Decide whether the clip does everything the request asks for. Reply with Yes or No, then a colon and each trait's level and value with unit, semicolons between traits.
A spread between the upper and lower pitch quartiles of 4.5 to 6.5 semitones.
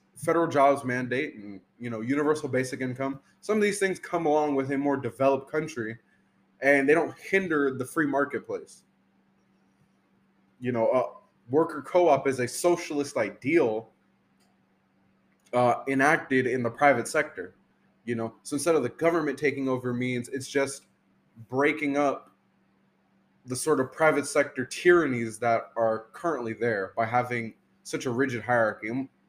No: average, 3.8 semitones